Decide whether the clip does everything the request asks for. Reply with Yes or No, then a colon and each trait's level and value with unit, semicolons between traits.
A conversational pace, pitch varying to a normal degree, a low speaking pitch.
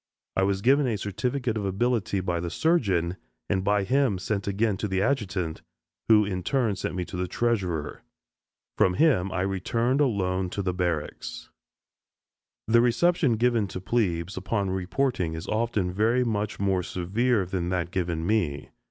Yes: average, 160 wpm; average, 4.3 semitones; low, 100 Hz